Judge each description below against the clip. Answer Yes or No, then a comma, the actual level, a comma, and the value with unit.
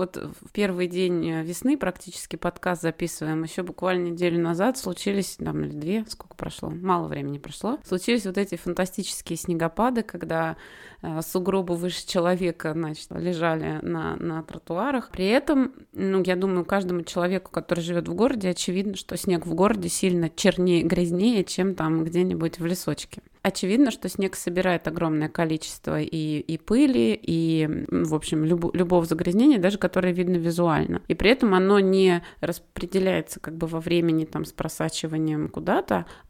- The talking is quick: No, average, 150 wpm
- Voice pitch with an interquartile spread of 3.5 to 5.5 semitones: No, narrow, 2.4 semitones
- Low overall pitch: No, medium, 175 Hz